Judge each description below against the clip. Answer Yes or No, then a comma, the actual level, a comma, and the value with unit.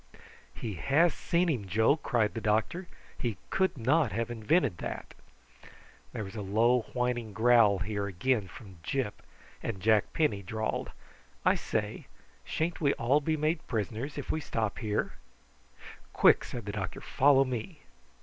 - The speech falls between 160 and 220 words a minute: No, average, 150 wpm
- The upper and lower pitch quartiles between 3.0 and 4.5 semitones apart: No, average, 5.0 semitones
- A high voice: No, low, 115 Hz